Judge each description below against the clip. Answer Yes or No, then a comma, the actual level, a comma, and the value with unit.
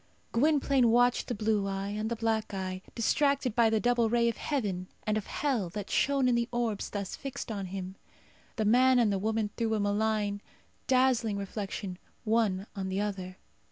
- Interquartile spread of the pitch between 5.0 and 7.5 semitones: No, average, 3.2 semitones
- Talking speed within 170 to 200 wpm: Yes, average, 185 wpm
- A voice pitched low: No, high, 220 Hz